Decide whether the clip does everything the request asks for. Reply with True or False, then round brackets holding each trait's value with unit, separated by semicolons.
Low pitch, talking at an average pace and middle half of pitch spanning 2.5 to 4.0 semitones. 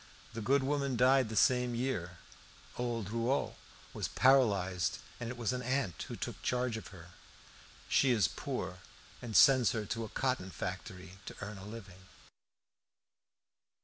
False (115 Hz; 150 wpm; 4.6 semitones)